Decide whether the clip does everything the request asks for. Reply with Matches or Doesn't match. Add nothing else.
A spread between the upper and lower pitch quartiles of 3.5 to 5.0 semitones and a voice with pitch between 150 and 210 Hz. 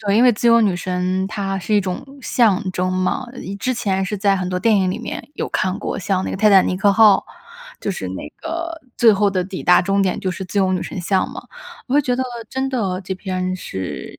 Doesn't match